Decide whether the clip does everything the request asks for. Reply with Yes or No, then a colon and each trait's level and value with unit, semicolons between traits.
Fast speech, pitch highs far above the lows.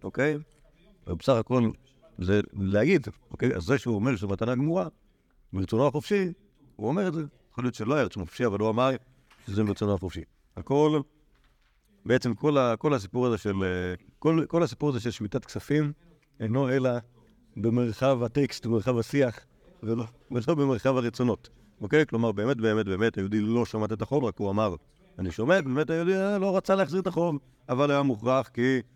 No: fast, 175 wpm; average, 5.0 semitones